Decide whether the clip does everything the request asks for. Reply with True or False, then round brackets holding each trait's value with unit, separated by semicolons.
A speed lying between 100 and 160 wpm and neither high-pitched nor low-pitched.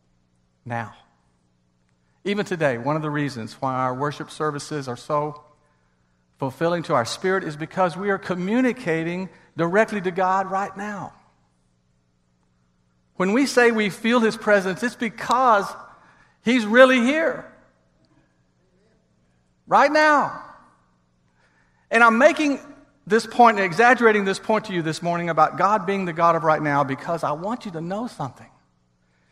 True (140 wpm; 160 Hz)